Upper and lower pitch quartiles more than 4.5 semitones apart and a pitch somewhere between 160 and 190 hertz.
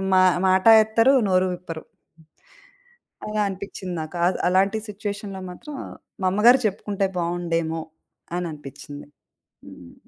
No: average, 3.2 semitones; medium, 185 Hz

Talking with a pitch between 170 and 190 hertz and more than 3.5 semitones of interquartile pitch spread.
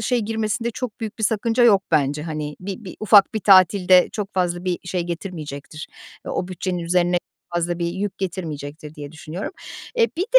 Yes: medium, 185 Hz; average, 3.9 semitones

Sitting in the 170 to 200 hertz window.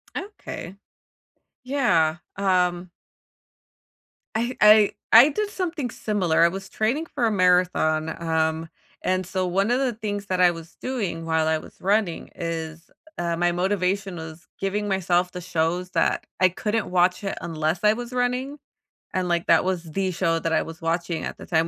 Yes: medium, 185 Hz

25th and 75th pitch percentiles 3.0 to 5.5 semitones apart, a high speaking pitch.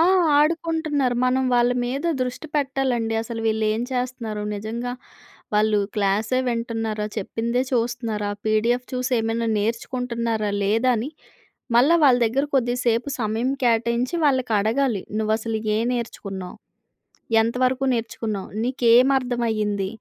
No: narrow, 2.5 semitones; high, 235 Hz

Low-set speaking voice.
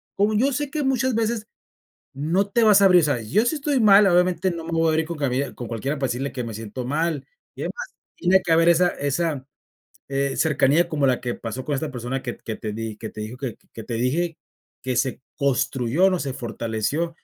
No: medium, 150 Hz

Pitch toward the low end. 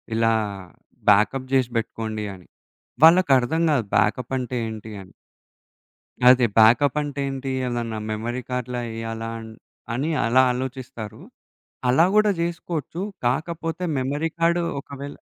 Yes: low, 125 Hz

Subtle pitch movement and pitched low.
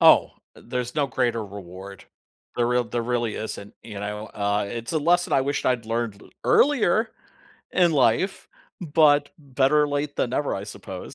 No: average, 5.2 semitones; low, 125 Hz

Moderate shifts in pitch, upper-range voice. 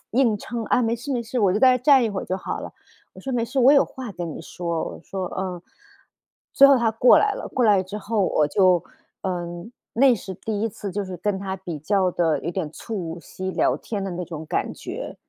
Yes: average, 4.6 semitones; high, 200 Hz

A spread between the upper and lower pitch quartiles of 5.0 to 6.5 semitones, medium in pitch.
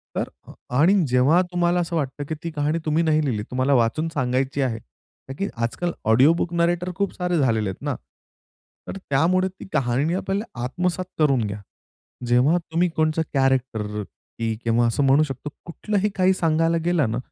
Yes: average, 5.3 semitones; medium, 150 Hz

